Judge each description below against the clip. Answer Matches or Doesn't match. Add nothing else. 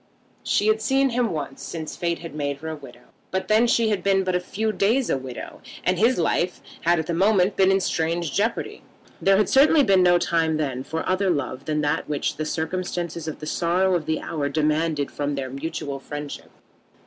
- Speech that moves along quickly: Matches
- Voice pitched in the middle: Matches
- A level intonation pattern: Doesn't match